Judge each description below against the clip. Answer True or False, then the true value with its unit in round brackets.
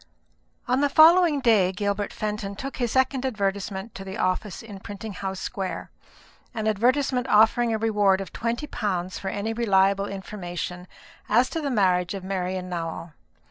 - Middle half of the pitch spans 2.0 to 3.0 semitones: False (3.7 semitones)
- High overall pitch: True (205 Hz)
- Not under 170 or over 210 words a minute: False (160 wpm)